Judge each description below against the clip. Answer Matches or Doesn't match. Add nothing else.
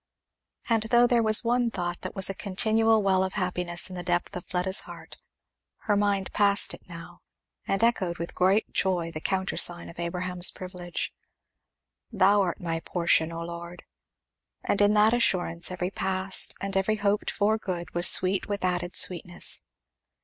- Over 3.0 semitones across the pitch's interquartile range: Doesn't match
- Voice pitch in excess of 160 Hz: Matches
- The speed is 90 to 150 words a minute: Doesn't match